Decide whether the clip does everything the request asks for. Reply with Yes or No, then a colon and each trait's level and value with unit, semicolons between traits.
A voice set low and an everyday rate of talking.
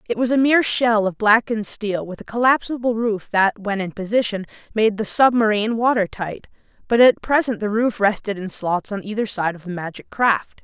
No: high, 215 Hz; average, 195 wpm